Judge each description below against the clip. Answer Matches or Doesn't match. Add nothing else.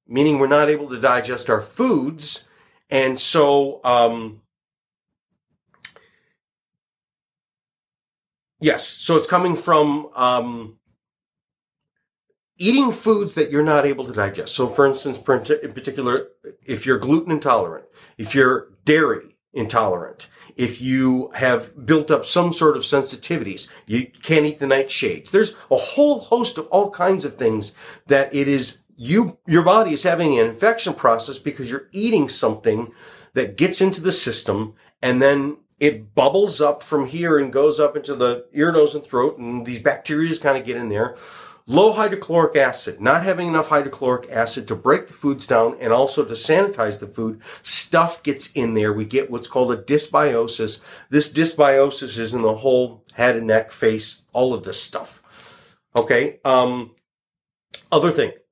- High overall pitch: Doesn't match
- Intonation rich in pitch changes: Doesn't match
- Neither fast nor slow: Matches